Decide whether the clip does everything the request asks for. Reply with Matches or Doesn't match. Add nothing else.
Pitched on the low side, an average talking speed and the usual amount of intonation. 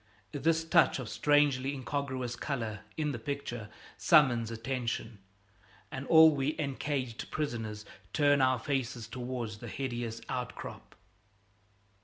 Doesn't match